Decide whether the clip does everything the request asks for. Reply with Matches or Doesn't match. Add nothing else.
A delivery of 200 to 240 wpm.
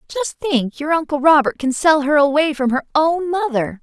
Matches